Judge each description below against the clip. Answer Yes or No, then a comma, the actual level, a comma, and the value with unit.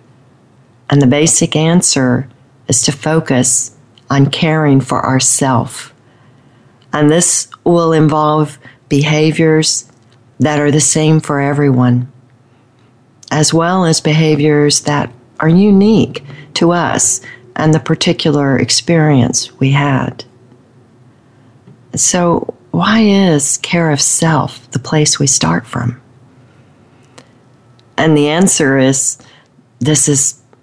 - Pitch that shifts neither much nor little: Yes, average, 3.5 semitones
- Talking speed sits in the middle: No, slow, 105 wpm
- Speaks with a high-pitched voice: No, medium, 140 Hz